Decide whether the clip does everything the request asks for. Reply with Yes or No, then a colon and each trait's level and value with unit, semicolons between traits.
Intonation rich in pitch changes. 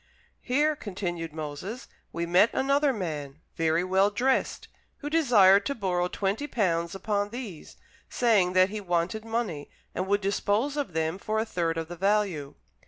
No: average, 4.9 semitones